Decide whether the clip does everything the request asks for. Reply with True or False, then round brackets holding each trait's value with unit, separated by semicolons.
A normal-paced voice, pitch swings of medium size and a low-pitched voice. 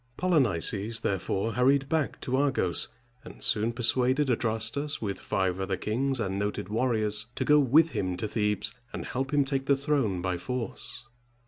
True (160 wpm; 4.8 semitones; 115 Hz)